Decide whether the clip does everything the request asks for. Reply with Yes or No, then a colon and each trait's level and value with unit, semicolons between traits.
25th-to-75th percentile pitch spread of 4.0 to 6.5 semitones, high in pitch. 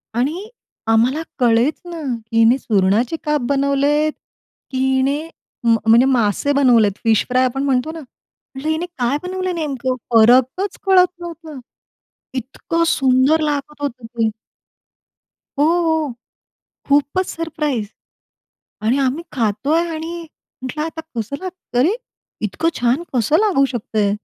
Yes: average, 4.7 semitones; very high, 275 Hz